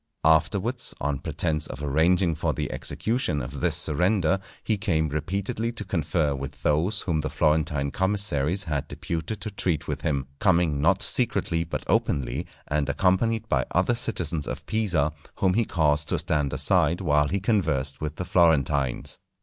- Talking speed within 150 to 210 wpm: Yes, average, 160 wpm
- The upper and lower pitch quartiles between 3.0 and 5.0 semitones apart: Yes, average, 4.6 semitones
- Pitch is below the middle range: Yes, very low, 80 Hz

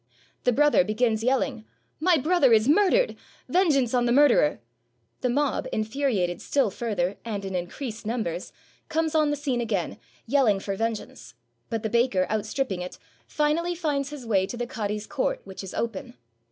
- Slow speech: No, average, 165 wpm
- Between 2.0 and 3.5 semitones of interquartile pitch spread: No, wide, 5.5 semitones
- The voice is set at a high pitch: Yes, high, 240 Hz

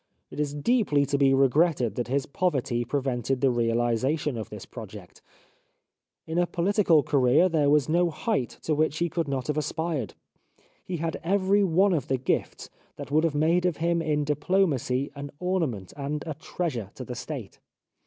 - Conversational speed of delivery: Yes, average, 175 wpm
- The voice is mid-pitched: Yes, medium, 150 Hz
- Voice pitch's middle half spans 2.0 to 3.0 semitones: No, average, 4.5 semitones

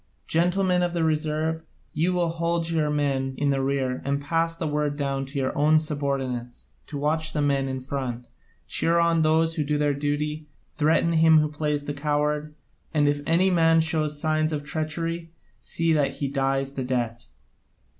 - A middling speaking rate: Yes, average, 180 wpm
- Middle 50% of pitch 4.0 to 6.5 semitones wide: No, narrow, 2.5 semitones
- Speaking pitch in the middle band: Yes, medium, 150 Hz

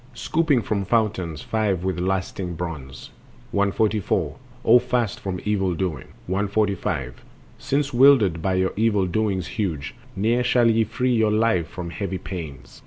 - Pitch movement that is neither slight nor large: Yes, average, 3.9 semitones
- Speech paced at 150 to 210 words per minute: No, average, 140 wpm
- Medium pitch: No, low, 100 Hz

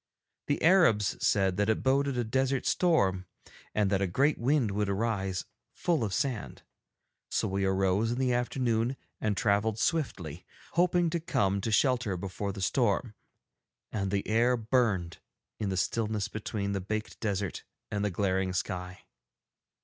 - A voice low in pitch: Yes, low, 105 Hz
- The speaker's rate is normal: Yes, average, 155 wpm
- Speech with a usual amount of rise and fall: Yes, average, 4.5 semitones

